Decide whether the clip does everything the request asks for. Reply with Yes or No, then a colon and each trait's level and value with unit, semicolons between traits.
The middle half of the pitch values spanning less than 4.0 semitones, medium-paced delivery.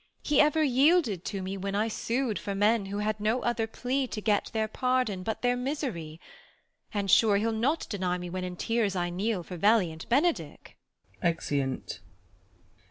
No: average, 4.9 semitones; average, 170 wpm